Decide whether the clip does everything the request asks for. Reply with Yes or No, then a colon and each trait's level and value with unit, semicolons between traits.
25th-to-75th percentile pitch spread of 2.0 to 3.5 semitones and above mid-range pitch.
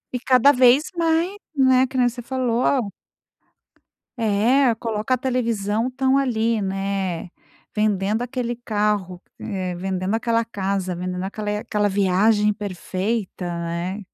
No: average, 4.3 semitones; high, 215 Hz